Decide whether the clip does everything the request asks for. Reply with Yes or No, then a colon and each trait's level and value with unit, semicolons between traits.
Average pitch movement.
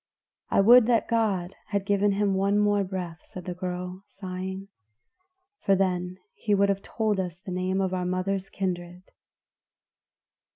No: narrow, 1.6 semitones